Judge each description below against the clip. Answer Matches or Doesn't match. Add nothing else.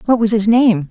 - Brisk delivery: Matches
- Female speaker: Doesn't match